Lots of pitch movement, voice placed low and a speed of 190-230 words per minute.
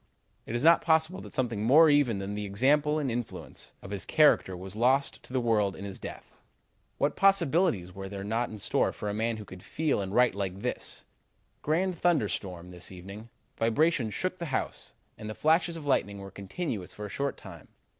Yes: wide, 7.4 semitones; low, 115 Hz; average, 200 wpm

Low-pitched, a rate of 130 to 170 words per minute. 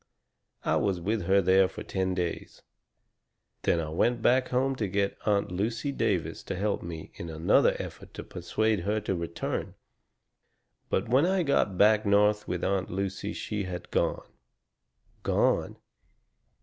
Yes: low, 100 Hz; average, 150 wpm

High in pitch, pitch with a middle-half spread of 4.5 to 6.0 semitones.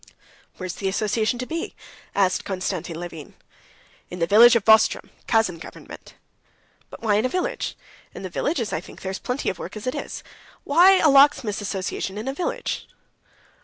Yes: high, 215 Hz; wide, 5.5 semitones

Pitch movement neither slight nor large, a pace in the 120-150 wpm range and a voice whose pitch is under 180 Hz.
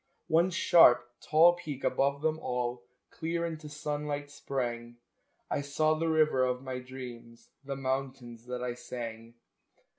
Yes: average, 3.9 semitones; average, 140 wpm; low, 135 Hz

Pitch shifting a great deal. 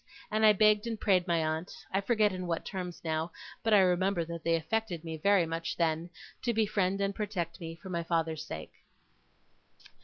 No: average, 3.7 semitones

